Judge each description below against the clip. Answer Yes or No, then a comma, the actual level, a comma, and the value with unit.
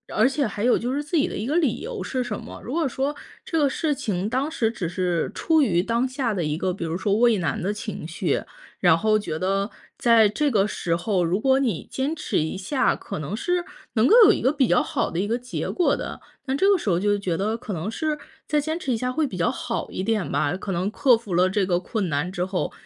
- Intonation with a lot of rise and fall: Yes, wide, 6.4 semitones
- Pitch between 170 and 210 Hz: No, high, 220 Hz